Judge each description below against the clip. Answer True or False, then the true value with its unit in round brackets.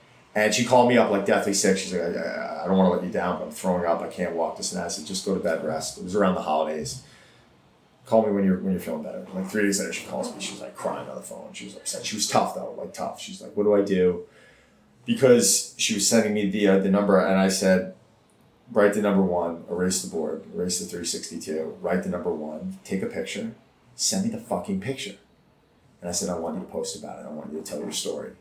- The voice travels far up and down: False (3.0 semitones)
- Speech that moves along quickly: True (275 wpm)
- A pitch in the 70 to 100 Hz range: True (95 Hz)